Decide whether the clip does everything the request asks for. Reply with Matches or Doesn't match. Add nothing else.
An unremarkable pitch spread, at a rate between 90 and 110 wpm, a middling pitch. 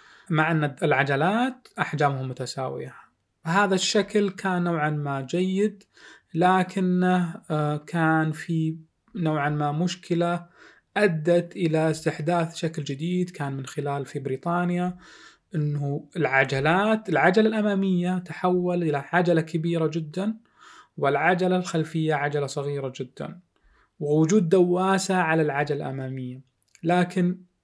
Matches